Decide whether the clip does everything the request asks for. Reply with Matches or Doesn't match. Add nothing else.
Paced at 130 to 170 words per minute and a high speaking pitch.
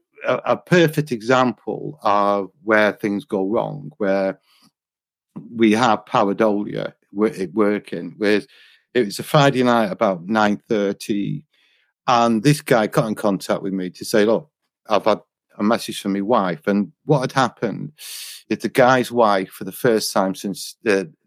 Doesn't match